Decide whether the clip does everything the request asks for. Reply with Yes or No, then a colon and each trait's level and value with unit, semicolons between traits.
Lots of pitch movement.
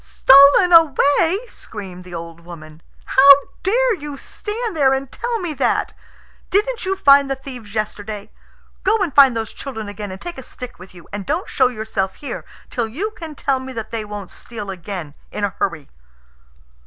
Yes: wide, 7.7 semitones